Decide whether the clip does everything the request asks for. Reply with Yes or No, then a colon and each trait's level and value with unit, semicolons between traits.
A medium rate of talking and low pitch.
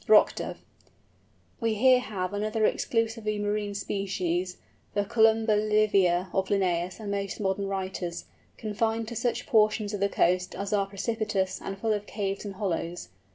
No: average, 155 wpm; high, 205 Hz